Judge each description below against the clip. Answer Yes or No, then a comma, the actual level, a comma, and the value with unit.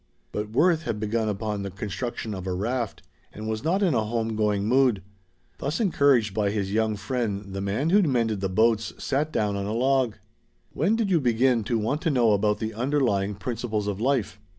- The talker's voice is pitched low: Yes, low, 110 Hz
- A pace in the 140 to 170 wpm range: No, average, 200 wpm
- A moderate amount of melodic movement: Yes, average, 4.2 semitones